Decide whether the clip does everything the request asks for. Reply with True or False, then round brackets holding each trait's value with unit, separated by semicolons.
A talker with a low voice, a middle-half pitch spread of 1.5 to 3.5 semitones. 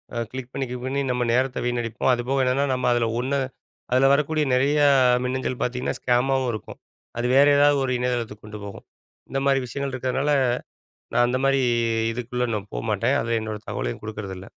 True (125 Hz; 2.4 semitones)